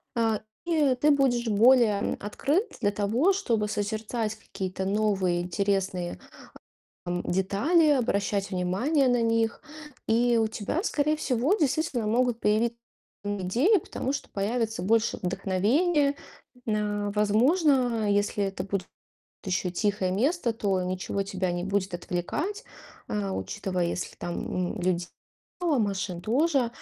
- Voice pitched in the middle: No, high, 215 Hz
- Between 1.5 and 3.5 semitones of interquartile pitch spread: No, average, 4.8 semitones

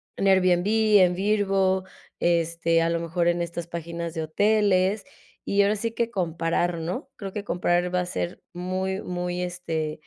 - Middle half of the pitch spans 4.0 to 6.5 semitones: No, narrow, 2.5 semitones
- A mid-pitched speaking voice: Yes, medium, 180 Hz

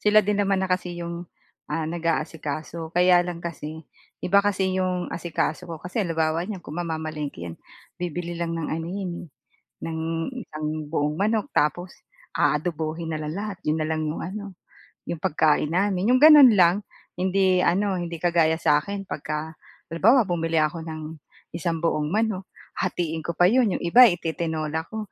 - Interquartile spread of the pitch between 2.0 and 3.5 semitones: Yes, average, 3.0 semitones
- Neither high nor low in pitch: Yes, medium, 170 Hz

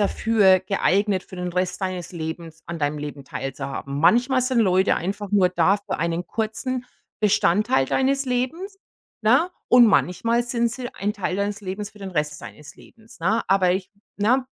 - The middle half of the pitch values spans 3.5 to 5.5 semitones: Yes, average, 4.9 semitones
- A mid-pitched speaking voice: No, high, 195 Hz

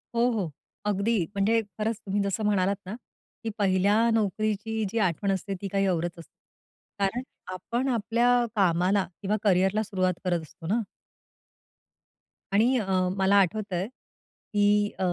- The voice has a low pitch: No, high, 200 Hz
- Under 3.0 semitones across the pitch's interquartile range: Yes, narrow, 2.4 semitones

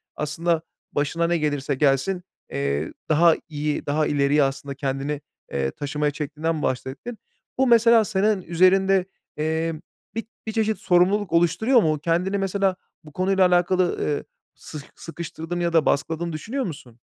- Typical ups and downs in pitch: Yes, average, 4.4 semitones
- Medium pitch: Yes, medium, 165 Hz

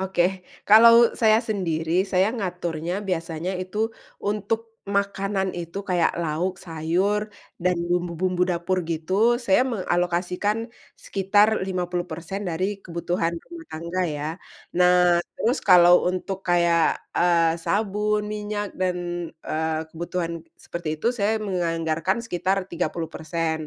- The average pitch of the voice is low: No, medium, 180 Hz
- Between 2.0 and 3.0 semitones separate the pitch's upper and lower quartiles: Yes, narrow, 2.6 semitones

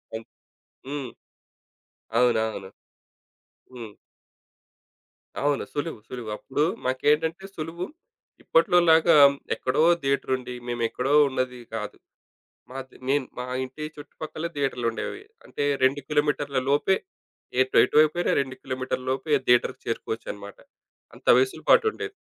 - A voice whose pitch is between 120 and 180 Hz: Yes, low, 135 Hz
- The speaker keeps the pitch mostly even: No, average, 3.5 semitones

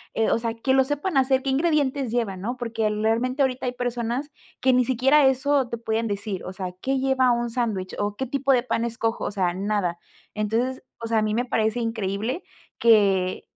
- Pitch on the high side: Yes, high, 235 Hz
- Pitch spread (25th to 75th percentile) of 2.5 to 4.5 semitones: Yes, average, 3.5 semitones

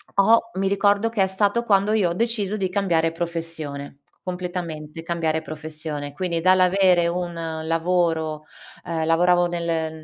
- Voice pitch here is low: No, medium, 175 Hz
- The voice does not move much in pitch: No, average, 3.0 semitones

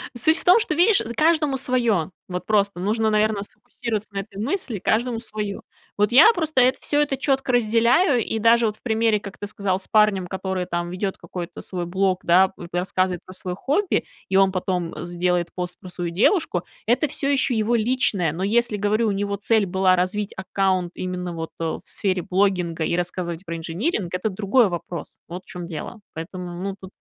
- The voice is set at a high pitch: Yes, high, 200 Hz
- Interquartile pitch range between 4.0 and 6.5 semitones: Yes, average, 4.5 semitones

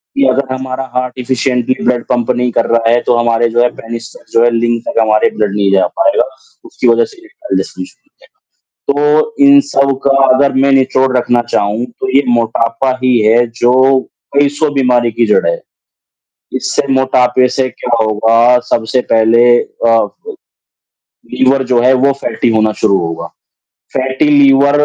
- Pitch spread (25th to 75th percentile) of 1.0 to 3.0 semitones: Yes, narrow, 2.6 semitones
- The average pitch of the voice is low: Yes, low, 125 Hz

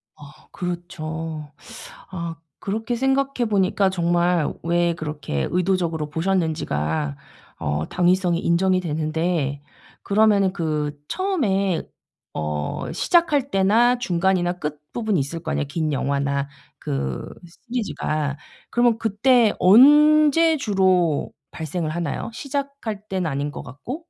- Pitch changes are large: Yes, wide, 5.9 semitones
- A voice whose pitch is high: No, medium, 175 Hz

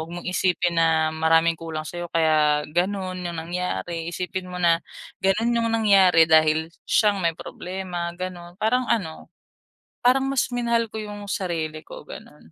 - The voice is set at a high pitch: No, medium, 175 Hz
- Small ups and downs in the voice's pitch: No, average, 3.4 semitones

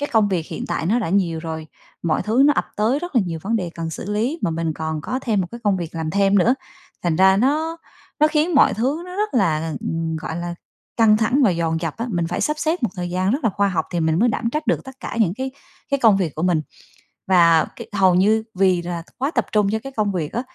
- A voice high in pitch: Yes, high, 195 Hz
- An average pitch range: No, wide, 6.4 semitones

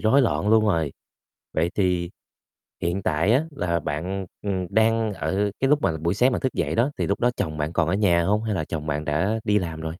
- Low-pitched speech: Yes, very low, 95 Hz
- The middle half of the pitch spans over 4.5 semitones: Yes, average, 4.9 semitones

